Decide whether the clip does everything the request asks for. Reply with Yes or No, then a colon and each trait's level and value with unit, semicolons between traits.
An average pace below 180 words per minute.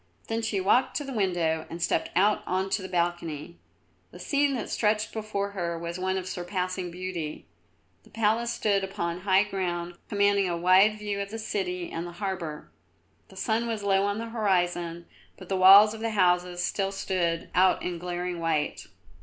No: average, 185 wpm